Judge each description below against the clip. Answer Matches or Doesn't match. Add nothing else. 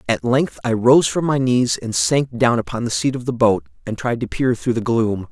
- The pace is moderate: Doesn't match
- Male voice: Matches